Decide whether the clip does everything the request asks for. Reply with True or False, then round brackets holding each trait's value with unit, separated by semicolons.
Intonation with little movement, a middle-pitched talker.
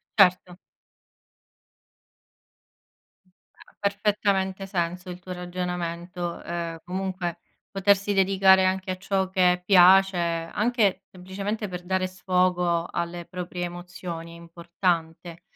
True (1.6 semitones; 180 Hz)